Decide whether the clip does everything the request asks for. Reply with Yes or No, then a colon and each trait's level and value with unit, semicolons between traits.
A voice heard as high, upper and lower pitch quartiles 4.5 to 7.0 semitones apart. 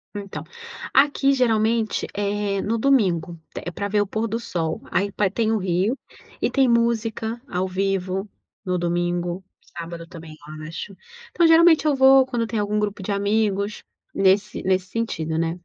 No: high, 205 Hz; average, 4.1 semitones